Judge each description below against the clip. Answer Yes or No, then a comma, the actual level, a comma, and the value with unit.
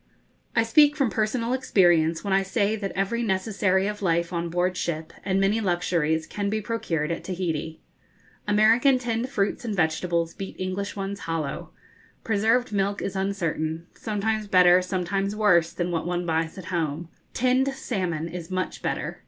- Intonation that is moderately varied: Yes, average, 3.9 semitones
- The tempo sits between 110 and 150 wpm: No, average, 160 wpm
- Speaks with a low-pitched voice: No, high, 190 Hz